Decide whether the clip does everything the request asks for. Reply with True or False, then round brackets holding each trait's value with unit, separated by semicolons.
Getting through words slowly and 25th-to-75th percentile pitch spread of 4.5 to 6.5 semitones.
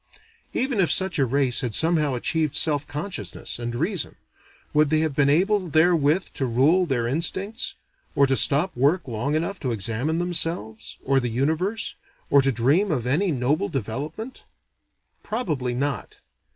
False (155 wpm; 5.1 semitones)